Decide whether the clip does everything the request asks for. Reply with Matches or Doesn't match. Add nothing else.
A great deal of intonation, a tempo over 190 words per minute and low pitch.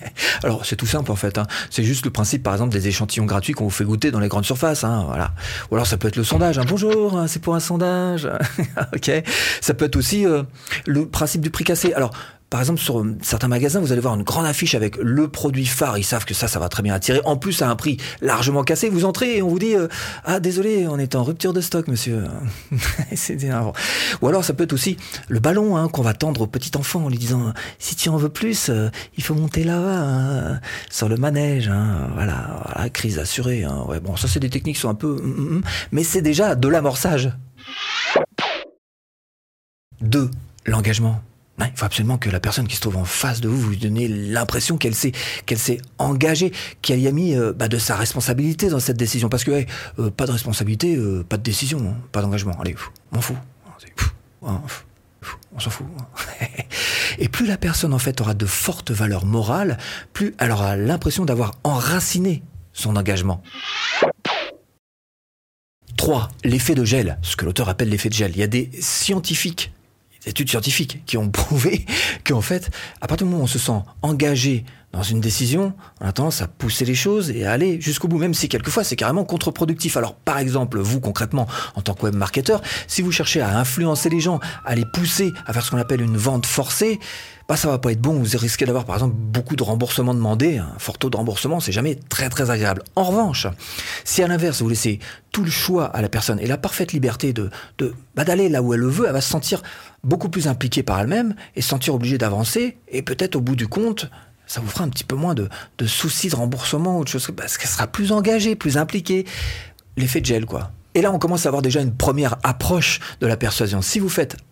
Matches